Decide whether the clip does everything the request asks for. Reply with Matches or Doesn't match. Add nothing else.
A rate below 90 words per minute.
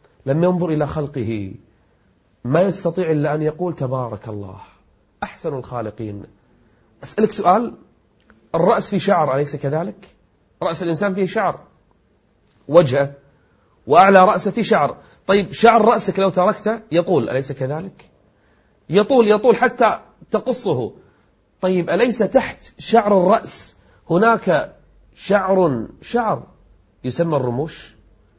Doesn't match